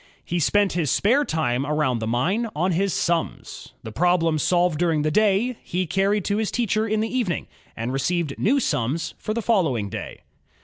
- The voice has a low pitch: No, medium, 175 Hz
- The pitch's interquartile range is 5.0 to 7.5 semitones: Yes, wide, 5.6 semitones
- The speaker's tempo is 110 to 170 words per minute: No, average, 185 wpm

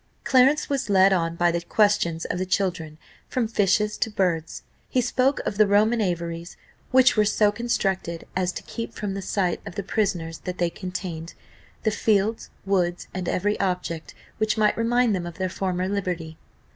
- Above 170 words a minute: Yes, average, 180 wpm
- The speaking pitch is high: Yes, high, 195 Hz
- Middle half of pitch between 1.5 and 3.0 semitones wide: No, average, 3.5 semitones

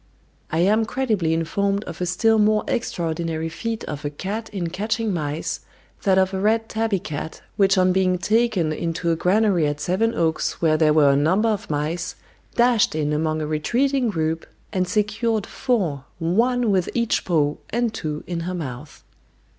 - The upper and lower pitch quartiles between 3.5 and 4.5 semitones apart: No, wide, 5.4 semitones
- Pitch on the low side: No, medium, 185 Hz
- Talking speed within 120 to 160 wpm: No, average, 170 wpm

